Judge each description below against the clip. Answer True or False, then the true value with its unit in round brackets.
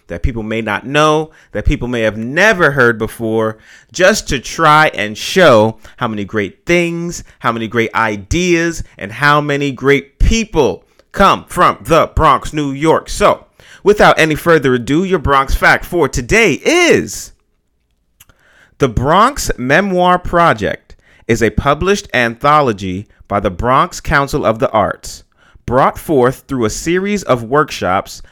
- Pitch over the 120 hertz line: True (135 Hz)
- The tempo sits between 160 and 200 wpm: False (145 wpm)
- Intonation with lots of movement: True (6.6 semitones)